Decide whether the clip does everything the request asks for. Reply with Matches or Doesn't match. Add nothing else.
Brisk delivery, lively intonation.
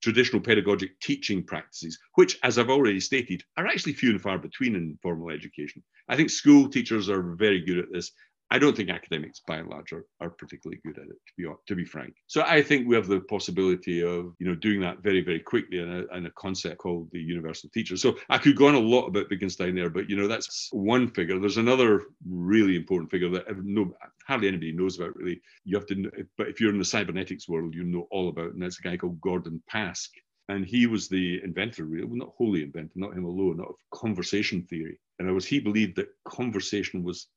Doesn't match